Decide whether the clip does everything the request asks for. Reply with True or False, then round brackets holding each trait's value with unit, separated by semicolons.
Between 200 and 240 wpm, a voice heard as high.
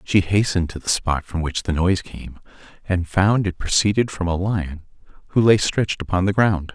False (205 wpm; 95 Hz)